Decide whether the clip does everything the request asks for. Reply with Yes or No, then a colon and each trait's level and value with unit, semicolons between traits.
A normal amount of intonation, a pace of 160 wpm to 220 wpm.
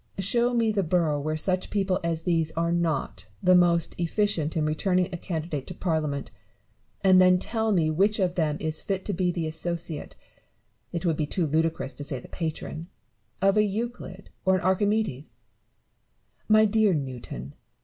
Yes: average, 3.6 semitones; average, 180 wpm